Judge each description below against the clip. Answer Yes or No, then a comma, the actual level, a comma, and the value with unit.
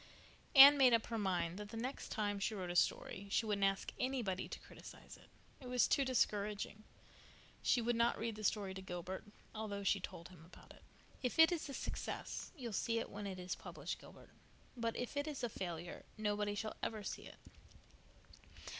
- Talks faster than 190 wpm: Yes, average, 200 wpm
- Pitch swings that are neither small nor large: Yes, average, 3.6 semitones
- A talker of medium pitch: No, high, 210 Hz